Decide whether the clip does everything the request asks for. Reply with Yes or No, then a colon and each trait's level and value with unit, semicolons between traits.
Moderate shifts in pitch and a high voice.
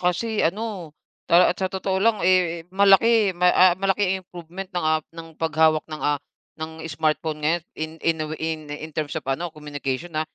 No: average, 3.1 semitones; medium, 165 Hz